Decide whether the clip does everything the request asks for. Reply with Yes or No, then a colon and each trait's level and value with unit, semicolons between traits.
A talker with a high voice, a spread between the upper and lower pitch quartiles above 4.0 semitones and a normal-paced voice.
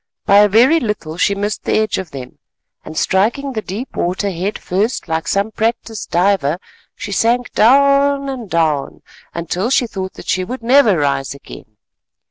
Yes: high, 205 Hz; average, 5.1 semitones; average, 170 wpm